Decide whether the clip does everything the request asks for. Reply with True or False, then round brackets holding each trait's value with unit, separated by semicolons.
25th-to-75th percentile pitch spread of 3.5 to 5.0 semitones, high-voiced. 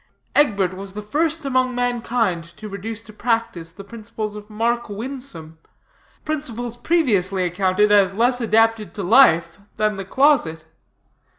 True (4.1 semitones; 215 Hz)